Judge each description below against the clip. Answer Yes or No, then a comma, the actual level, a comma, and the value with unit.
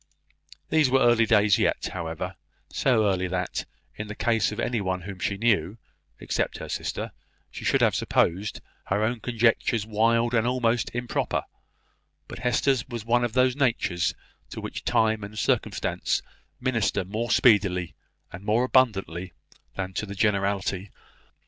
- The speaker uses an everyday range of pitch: Yes, average, 3.5 semitones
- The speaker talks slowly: No, average, 150 wpm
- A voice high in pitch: No, low, 110 Hz